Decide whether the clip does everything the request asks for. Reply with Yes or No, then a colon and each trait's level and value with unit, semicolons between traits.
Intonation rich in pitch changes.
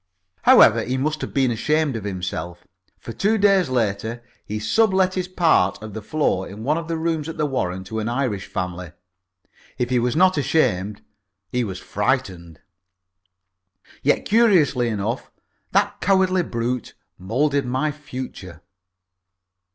Yes: wide, 7.2 semitones